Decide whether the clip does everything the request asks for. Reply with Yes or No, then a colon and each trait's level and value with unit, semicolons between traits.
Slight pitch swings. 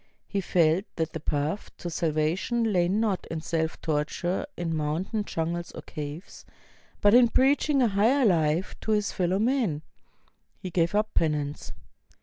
No: average, 4.9 semitones